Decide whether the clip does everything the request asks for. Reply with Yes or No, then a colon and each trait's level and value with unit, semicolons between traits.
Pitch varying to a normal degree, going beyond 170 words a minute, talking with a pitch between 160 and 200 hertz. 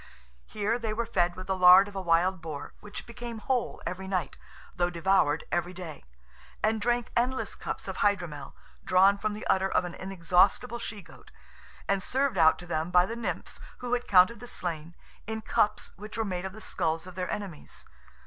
Yes: average, 3.5 semitones; average, 195 wpm; high, 190 Hz